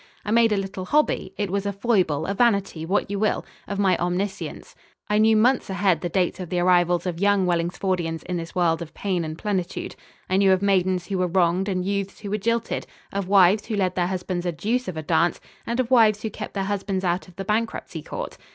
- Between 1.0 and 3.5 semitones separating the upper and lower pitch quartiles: Yes, narrow, 2.5 semitones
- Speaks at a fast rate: Yes, fast, 230 wpm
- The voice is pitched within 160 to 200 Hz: Yes, high, 190 Hz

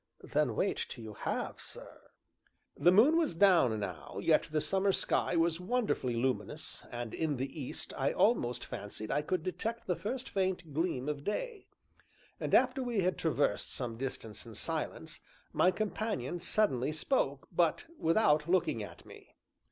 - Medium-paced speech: Yes, average, 160 wpm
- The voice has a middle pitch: Yes, medium, 165 Hz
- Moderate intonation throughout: No, wide, 7.6 semitones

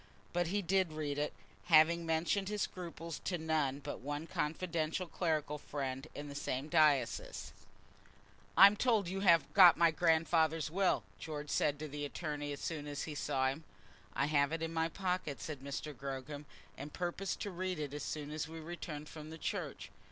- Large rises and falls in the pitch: No, average, 2.8 semitones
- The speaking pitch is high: No, medium, 155 Hz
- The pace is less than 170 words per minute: No, average, 180 wpm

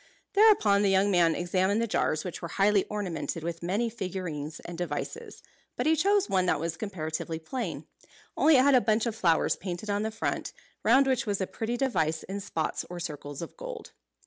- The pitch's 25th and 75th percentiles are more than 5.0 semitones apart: Yes, wide, 5.6 semitones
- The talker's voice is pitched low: No, high, 195 Hz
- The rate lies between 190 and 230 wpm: Yes, average, 200 wpm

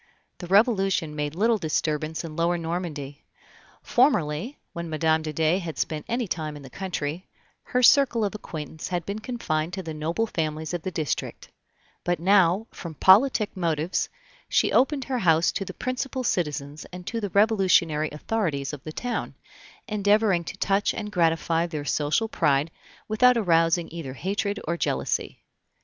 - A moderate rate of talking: Yes, average, 160 wpm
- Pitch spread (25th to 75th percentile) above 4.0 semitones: Yes, average, 4.9 semitones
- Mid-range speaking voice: Yes, medium, 175 Hz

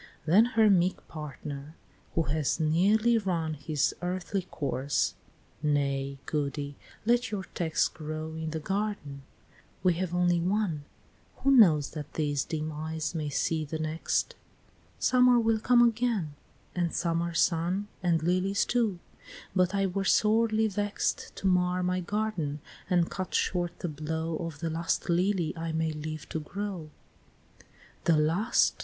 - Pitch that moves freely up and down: No, average, 4.1 semitones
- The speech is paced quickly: No, average, 145 wpm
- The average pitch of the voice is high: No, medium, 170 Hz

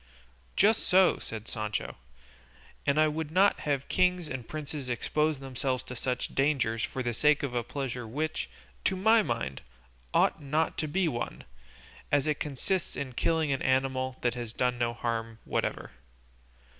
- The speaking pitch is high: No, low, 135 Hz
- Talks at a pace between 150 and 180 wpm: Yes, average, 160 wpm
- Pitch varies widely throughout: No, average, 4.2 semitones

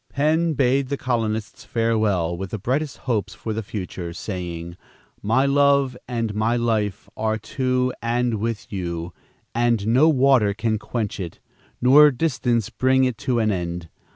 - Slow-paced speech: No, average, 155 wpm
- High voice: No, low, 115 Hz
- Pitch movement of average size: Yes, average, 4.1 semitones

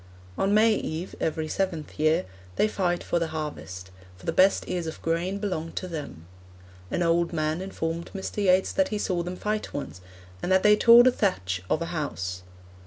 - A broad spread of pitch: No, average, 3.7 semitones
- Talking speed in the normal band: Yes, average, 190 wpm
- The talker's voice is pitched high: No, medium, 170 Hz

